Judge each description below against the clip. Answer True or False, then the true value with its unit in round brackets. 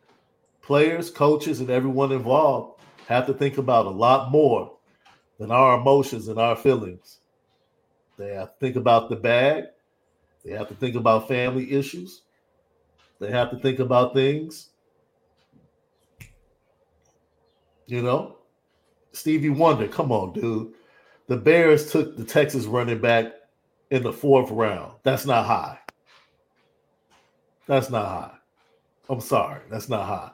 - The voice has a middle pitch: False (125 Hz)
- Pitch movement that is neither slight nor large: True (3.4 semitones)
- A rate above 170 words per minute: False (135 wpm)